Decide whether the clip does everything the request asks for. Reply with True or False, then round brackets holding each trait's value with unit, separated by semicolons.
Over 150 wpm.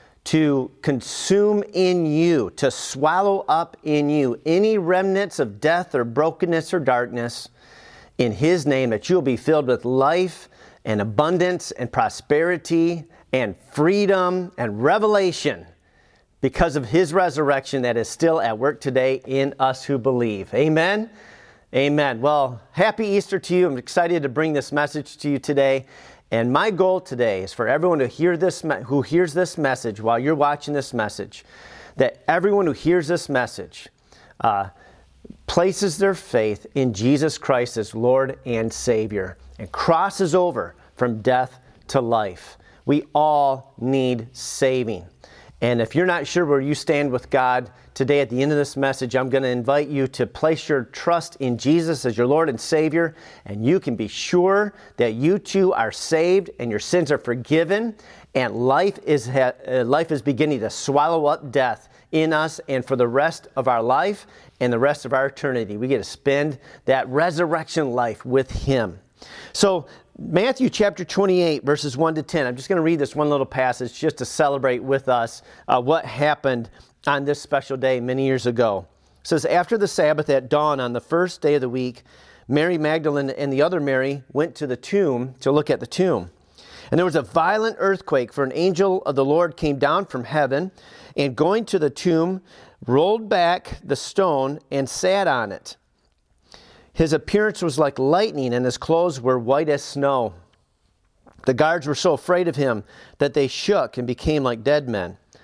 True (175 wpm)